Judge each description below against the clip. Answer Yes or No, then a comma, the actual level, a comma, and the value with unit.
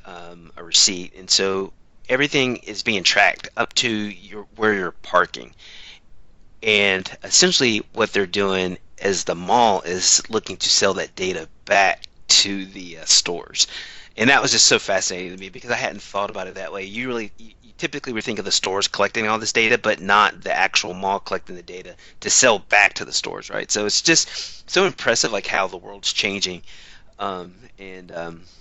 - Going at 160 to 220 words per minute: Yes, average, 190 wpm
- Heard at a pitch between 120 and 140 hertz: No, low, 100 Hz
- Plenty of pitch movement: No, average, 3.1 semitones